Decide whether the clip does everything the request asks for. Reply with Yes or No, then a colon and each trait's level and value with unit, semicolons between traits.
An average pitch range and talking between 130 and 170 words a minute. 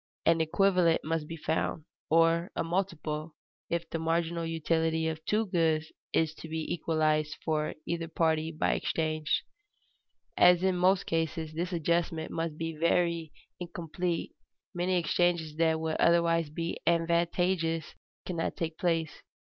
No: narrow, 1.2 semitones; slow, 135 wpm